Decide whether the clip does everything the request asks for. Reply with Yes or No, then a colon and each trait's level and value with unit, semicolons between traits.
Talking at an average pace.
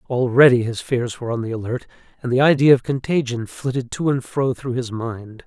No: fast, 210 wpm